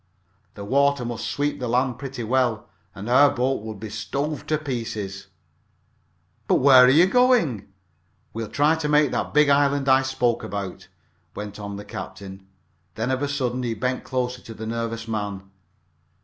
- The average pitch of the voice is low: Yes, low, 125 Hz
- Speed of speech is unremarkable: Yes, average, 170 wpm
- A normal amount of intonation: Yes, average, 4.6 semitones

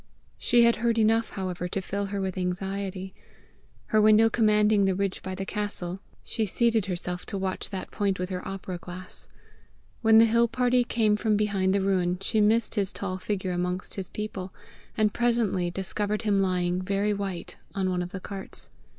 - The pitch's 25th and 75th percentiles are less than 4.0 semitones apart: Yes, narrow, 2.5 semitones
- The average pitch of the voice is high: Yes, high, 195 Hz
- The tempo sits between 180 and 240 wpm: Yes, average, 185 wpm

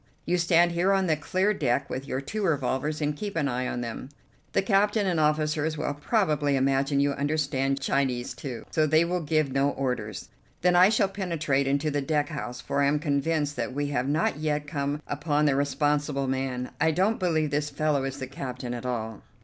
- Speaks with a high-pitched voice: No, medium, 145 Hz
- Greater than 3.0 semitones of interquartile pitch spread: No, average, 2.7 semitones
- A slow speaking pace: No, fast, 205 wpm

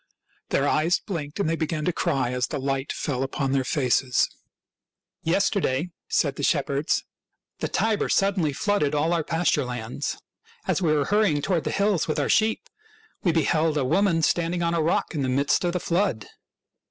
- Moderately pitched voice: Yes, medium, 155 Hz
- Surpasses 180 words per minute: Yes, average, 190 wpm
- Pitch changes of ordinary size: Yes, average, 4.2 semitones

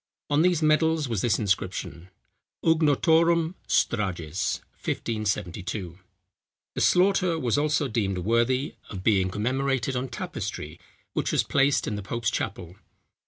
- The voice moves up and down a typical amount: No, wide, 7.5 semitones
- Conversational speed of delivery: No, slow, 120 wpm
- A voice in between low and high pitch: No, low, 120 Hz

